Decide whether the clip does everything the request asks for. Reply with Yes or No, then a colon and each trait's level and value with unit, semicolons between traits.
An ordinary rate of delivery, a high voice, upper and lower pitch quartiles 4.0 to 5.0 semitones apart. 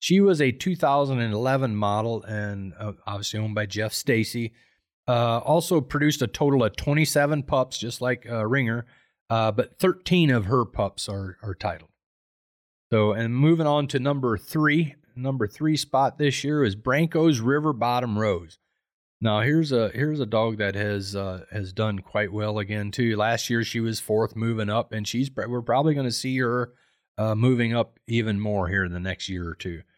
No: average, 185 wpm; low, 115 Hz; average, 4.6 semitones